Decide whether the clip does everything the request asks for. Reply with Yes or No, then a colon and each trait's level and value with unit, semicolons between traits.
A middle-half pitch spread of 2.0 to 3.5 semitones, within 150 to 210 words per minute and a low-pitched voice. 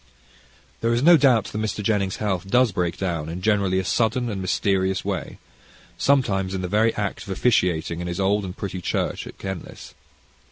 Yes: average, 3.0 semitones; average, 190 wpm; very low, 95 Hz